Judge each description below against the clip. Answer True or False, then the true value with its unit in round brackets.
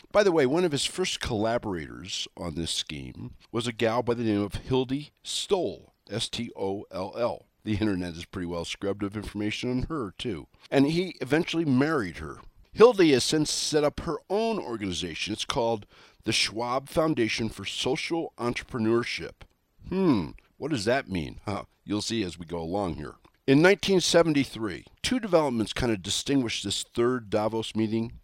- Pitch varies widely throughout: True (5.7 semitones)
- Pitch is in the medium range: False (115 Hz)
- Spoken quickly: False (165 wpm)